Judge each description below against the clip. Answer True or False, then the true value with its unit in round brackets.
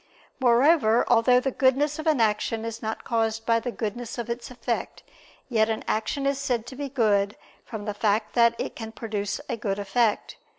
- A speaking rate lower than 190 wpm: False (195 wpm)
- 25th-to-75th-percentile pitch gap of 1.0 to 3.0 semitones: True (2.5 semitones)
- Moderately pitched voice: False (230 Hz)